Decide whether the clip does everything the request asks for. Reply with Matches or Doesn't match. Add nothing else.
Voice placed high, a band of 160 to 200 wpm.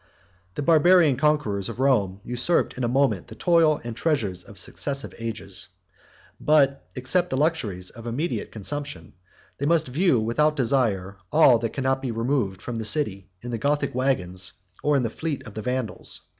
Doesn't match